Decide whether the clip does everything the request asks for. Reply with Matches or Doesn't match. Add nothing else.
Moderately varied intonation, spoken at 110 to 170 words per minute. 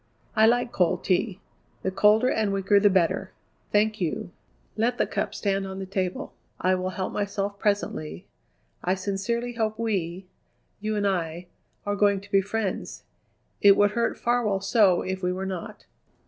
Doesn't match